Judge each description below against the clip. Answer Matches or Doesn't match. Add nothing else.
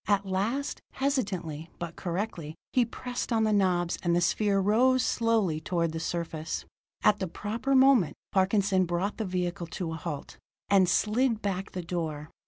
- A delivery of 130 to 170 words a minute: Matches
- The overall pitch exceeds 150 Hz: Matches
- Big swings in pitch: Doesn't match